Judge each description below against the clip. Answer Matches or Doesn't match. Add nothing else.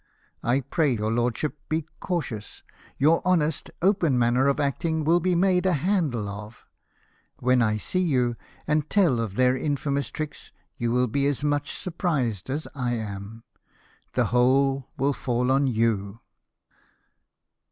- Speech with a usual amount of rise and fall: Matches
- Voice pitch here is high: Doesn't match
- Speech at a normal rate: Matches